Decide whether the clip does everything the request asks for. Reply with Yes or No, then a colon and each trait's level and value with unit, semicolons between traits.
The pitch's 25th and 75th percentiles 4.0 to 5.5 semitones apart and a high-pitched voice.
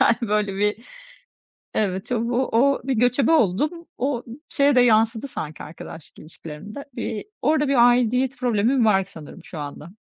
Yes: average, 4.6 semitones; high, 235 Hz